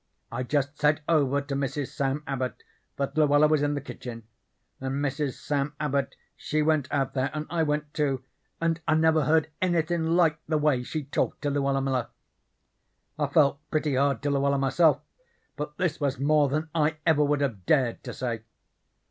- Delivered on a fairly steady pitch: Yes, narrow, 2.0 semitones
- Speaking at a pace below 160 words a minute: No, average, 180 wpm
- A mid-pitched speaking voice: Yes, medium, 145 Hz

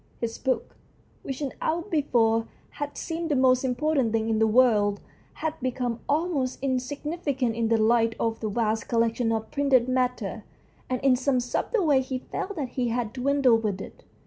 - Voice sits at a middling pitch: No, very high, 250 Hz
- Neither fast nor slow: Yes, average, 175 wpm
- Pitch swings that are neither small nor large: Yes, average, 3.6 semitones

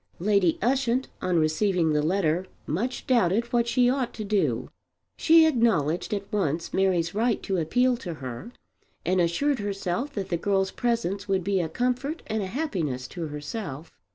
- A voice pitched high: Yes, high, 195 Hz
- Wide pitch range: Yes, wide, 5.8 semitones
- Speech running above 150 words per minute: Yes, average, 165 wpm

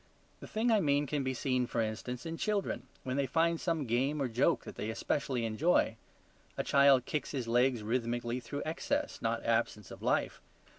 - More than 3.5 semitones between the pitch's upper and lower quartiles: Yes, average, 4.2 semitones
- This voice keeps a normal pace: Yes, average, 190 wpm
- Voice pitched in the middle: No, low, 130 Hz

